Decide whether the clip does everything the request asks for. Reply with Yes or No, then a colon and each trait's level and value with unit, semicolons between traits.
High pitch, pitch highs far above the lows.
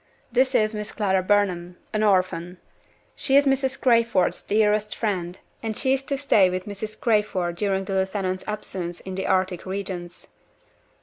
No: high, 200 Hz; average, 2.8 semitones